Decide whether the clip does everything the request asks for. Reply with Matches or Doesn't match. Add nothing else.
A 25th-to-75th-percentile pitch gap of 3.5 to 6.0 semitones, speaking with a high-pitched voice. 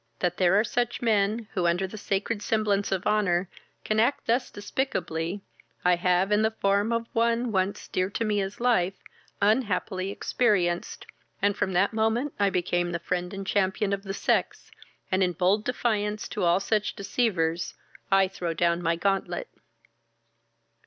Doesn't match